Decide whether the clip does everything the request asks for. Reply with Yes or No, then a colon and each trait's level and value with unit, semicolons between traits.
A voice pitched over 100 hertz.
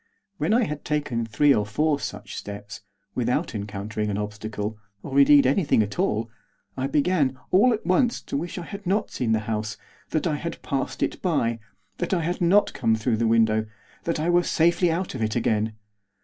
Yes: low, 135 Hz